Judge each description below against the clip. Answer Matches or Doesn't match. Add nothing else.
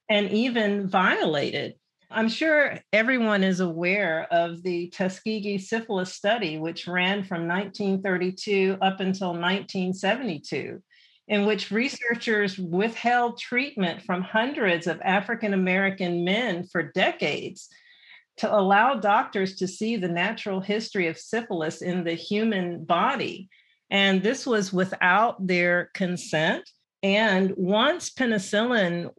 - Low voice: Doesn't match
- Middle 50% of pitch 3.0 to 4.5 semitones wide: Matches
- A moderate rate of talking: Doesn't match